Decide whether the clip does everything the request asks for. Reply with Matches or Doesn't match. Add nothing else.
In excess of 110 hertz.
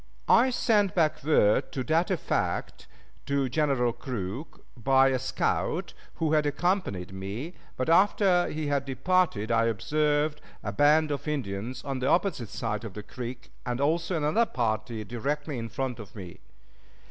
Matches